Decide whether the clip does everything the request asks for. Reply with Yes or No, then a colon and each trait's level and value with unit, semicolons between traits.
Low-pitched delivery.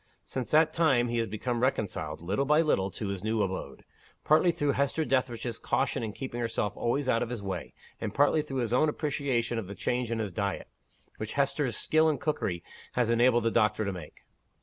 Yes: low, 120 Hz